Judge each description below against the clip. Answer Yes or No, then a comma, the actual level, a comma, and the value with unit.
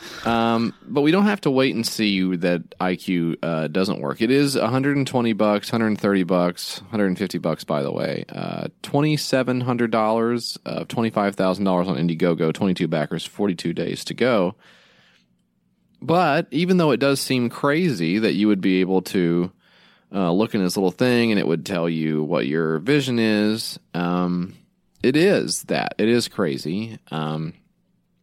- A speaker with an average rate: Yes, average, 155 wpm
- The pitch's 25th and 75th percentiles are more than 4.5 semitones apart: Yes, wide, 5.5 semitones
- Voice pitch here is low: Yes, low, 105 Hz